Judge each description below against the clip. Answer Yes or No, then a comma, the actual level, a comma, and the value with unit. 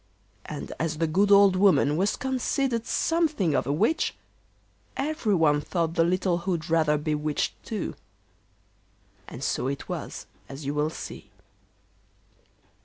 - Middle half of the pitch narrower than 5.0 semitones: No, average, 5.3 semitones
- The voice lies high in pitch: No, medium, 170 Hz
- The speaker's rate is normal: No, slow, 130 wpm